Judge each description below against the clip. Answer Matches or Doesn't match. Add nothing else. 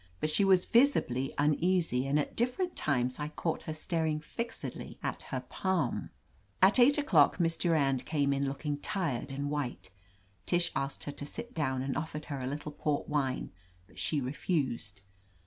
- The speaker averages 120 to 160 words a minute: Doesn't match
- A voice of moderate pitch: Matches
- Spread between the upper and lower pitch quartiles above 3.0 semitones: Matches